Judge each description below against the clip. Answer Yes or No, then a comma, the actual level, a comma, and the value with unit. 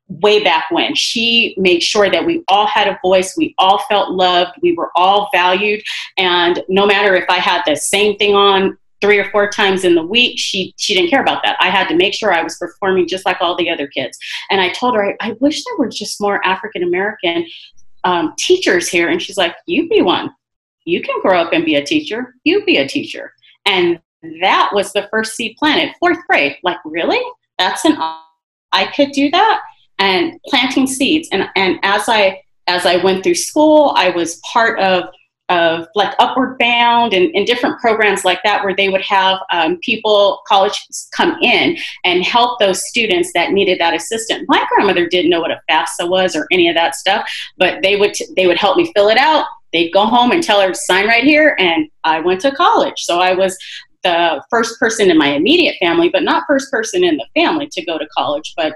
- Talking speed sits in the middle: No, fast, 215 wpm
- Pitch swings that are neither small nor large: No, wide, 8.4 semitones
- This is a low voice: No, high, 205 Hz